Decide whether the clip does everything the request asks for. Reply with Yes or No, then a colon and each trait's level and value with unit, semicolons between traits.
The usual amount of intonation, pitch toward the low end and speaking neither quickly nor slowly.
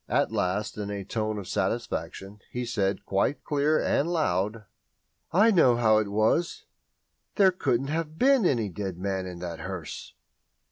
No: wide, 7.5 semitones; low, 110 Hz; average, 155 wpm